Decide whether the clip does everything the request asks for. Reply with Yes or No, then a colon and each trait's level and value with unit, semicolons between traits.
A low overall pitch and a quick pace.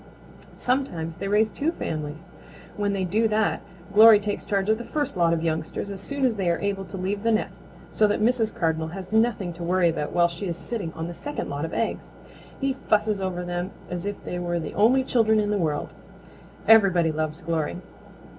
No: high, 195 Hz; fast, 210 wpm